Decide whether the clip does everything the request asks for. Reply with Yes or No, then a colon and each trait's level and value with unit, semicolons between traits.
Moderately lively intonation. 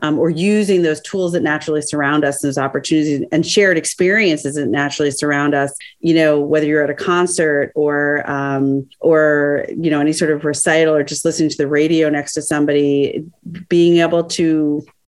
No: narrow, 2.2 semitones